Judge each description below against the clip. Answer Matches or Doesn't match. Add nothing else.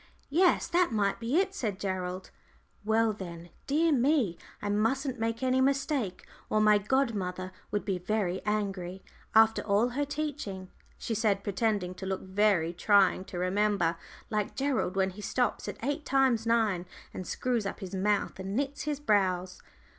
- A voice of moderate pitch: Doesn't match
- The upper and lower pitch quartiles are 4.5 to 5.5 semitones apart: Matches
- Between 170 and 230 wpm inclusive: Doesn't match